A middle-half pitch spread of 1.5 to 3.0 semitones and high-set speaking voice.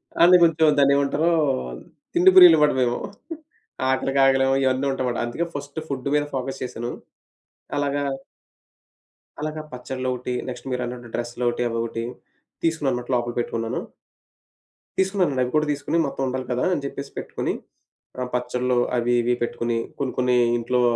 No: average, 2.7 semitones; low, 130 Hz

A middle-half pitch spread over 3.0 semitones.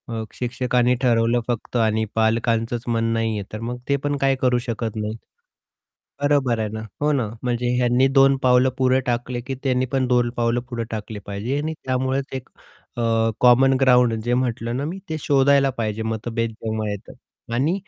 No: narrow, 2.5 semitones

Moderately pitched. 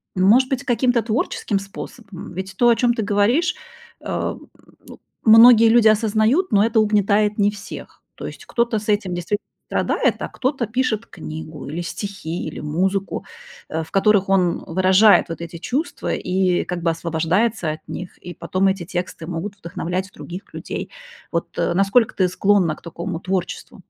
No: high, 195 Hz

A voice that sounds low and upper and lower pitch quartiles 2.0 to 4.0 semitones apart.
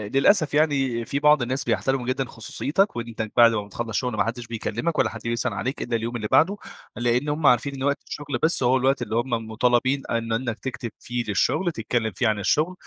Yes: low, 125 Hz; average, 3.2 semitones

